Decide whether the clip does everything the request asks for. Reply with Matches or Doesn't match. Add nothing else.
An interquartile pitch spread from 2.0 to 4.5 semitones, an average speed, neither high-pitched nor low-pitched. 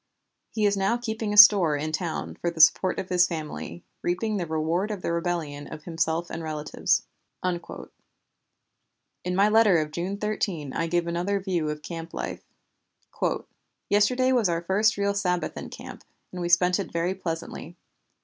Matches